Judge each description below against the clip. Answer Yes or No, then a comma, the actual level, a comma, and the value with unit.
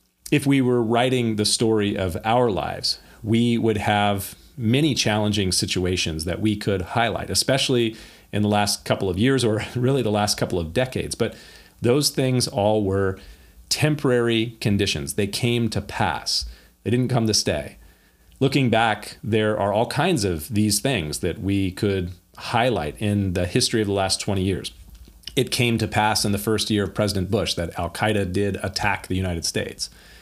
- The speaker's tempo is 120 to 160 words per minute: No, average, 175 wpm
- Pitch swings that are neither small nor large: Yes, average, 3.7 semitones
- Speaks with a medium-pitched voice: No, low, 105 Hz